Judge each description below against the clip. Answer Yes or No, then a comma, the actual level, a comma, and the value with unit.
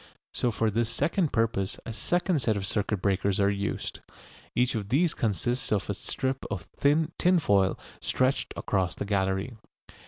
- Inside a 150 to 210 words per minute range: Yes, average, 160 wpm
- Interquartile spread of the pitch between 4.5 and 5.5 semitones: Yes, average, 4.9 semitones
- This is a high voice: No, low, 110 Hz